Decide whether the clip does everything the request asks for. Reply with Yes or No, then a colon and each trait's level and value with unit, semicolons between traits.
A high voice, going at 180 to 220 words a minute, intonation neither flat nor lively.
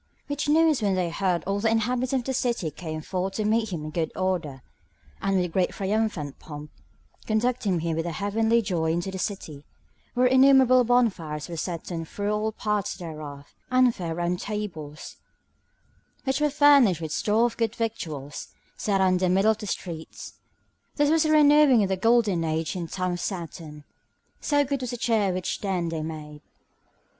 No: high, 195 Hz; average, 190 wpm; wide, 6.0 semitones